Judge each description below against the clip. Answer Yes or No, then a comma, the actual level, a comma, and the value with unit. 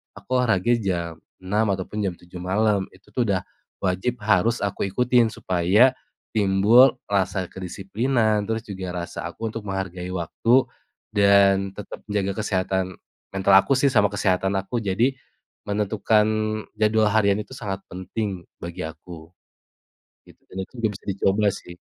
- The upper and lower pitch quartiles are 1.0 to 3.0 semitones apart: Yes, narrow, 2.6 semitones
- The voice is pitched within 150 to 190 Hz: No, low, 100 Hz